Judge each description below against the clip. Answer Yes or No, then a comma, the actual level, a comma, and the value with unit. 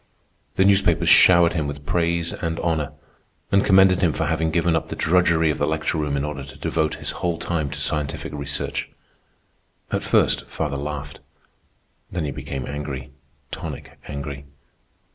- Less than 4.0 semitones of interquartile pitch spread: Yes, average, 3.0 semitones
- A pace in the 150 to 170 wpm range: Yes, average, 160 wpm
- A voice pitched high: No, very low, 75 Hz